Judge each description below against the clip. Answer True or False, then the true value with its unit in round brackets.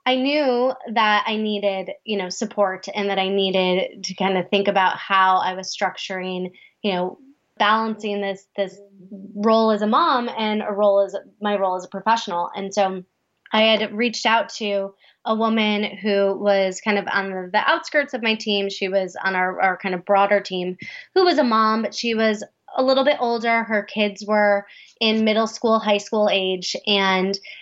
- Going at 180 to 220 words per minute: True (190 wpm)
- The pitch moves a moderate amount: False (2.3 semitones)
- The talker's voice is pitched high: True (205 Hz)